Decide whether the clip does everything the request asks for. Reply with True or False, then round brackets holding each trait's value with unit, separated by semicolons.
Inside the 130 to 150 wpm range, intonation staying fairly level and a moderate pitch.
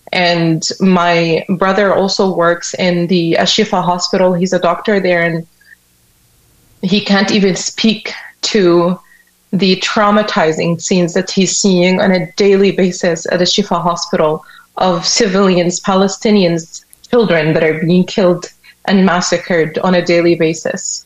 True (135 wpm; 2.3 semitones; 180 Hz)